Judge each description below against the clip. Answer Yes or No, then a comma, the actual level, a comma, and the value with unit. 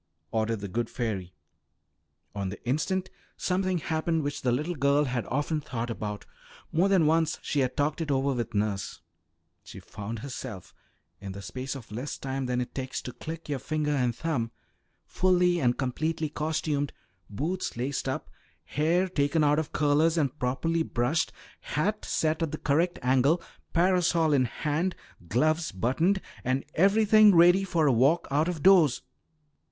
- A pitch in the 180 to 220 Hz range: No, medium, 145 Hz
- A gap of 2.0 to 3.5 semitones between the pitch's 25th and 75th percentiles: No, average, 4.7 semitones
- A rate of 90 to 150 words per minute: No, average, 160 wpm